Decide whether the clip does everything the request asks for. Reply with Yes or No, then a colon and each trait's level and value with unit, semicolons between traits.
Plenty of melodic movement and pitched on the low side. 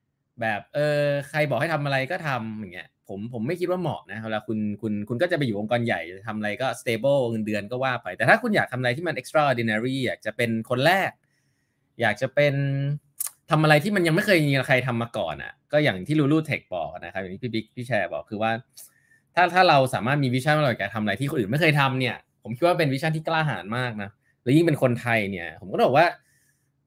No: average, 4.7 semitones; low, 130 Hz